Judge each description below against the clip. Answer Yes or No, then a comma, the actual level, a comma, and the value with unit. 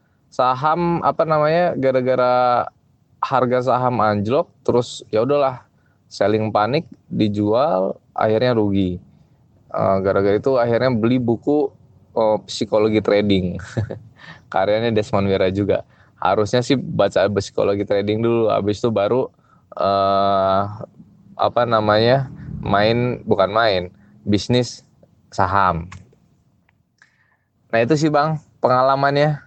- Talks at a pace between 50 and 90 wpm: No, average, 100 wpm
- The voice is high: No, low, 115 Hz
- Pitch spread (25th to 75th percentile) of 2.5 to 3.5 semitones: No, average, 4.4 semitones